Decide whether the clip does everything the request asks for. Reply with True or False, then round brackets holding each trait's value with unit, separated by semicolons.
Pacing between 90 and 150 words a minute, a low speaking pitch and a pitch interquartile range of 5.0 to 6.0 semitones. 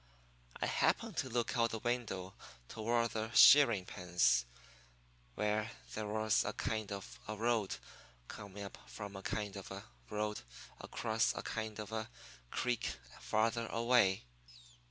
False (140 wpm; 110 Hz; 2.4 semitones)